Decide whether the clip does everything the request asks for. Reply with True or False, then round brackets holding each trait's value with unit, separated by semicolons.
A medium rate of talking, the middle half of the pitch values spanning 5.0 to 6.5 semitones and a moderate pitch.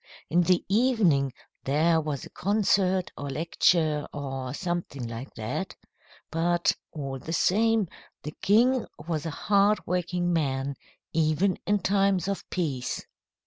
False (125 wpm; 5.3 semitones; 170 Hz)